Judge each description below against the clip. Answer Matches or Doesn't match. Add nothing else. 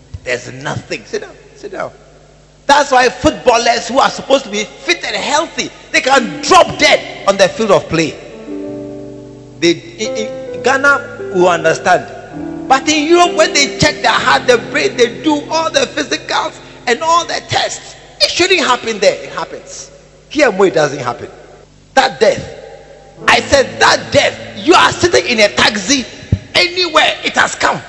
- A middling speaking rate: Matches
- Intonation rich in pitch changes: Matches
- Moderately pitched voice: Doesn't match